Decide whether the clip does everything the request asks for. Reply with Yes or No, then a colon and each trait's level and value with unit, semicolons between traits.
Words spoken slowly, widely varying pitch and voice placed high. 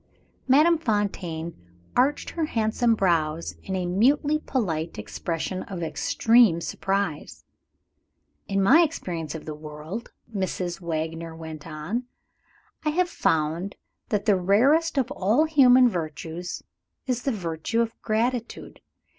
Yes: slow, 120 wpm; wide, 7.1 semitones; high, 195 Hz